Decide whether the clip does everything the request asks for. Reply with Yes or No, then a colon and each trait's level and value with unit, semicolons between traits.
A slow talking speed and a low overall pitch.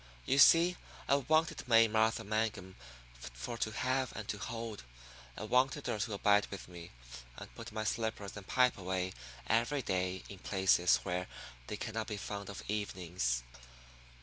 No: average, 160 wpm; low, 105 Hz